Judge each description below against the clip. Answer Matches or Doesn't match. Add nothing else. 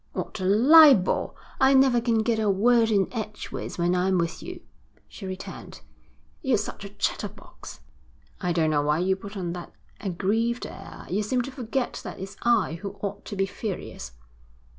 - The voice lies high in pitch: Matches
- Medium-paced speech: Matches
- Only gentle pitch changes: Doesn't match